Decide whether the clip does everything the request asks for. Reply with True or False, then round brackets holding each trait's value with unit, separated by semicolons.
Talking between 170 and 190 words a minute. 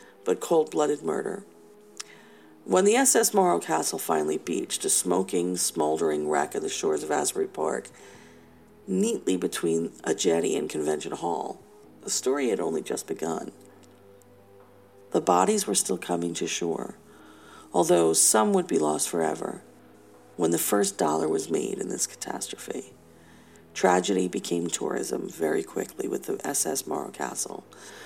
False (140 wpm)